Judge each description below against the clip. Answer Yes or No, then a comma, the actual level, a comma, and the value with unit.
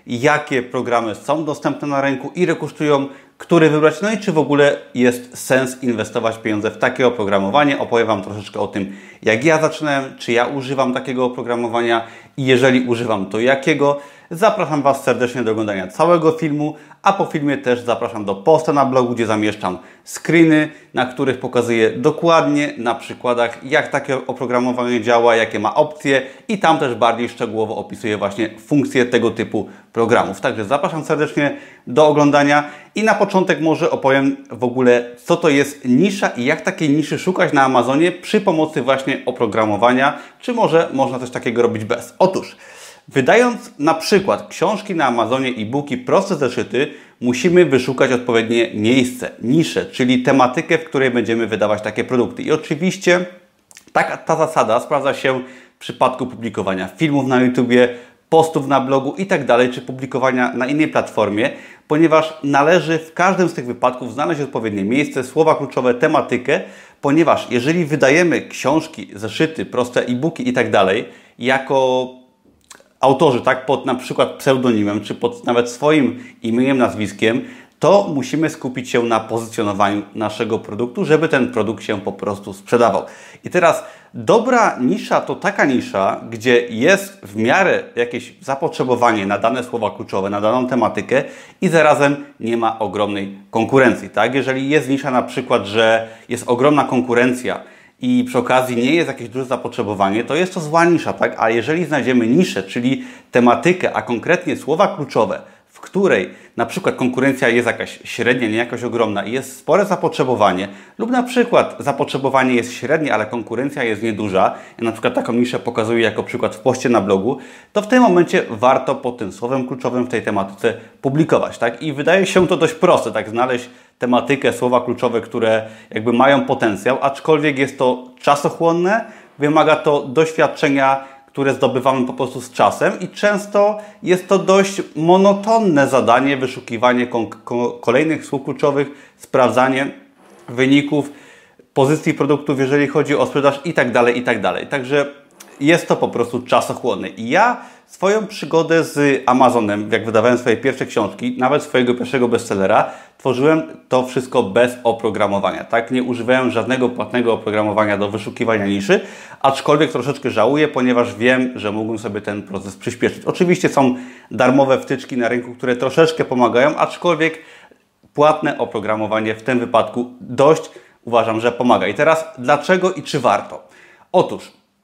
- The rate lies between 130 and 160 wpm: Yes, average, 155 wpm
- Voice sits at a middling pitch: No, low, 130 Hz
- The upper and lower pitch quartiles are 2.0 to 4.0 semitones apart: No, average, 4.4 semitones